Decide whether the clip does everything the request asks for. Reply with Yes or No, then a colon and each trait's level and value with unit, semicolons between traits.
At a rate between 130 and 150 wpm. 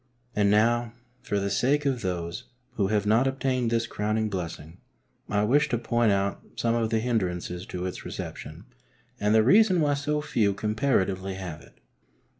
No: average, 170 wpm